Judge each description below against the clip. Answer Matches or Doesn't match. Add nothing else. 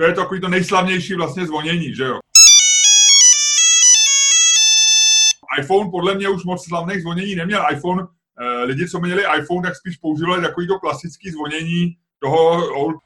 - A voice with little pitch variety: Doesn't match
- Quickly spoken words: Doesn't match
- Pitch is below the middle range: Doesn't match